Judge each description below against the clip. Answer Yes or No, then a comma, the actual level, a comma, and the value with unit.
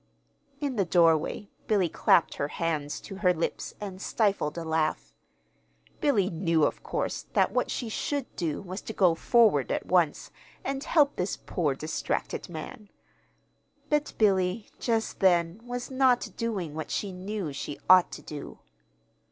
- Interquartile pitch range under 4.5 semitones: No, average, 5.2 semitones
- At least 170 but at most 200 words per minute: No, average, 150 wpm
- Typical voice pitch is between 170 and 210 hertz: Yes, medium, 185 Hz